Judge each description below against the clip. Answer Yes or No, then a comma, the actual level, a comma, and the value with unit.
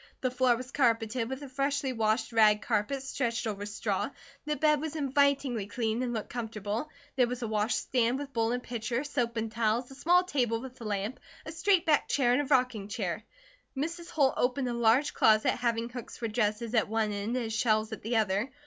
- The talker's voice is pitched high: Yes, high, 240 Hz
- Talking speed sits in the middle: No, fast, 210 wpm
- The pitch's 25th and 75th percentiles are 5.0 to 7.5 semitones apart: No, average, 3.3 semitones